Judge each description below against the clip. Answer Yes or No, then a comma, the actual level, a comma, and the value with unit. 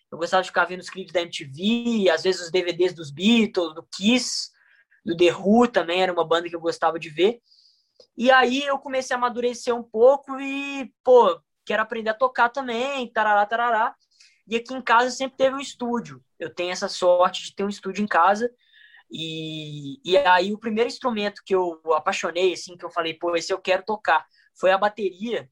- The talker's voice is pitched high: Yes, high, 195 Hz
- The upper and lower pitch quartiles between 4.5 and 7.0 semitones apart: Yes, wide, 5.5 semitones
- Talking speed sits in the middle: No, fast, 200 wpm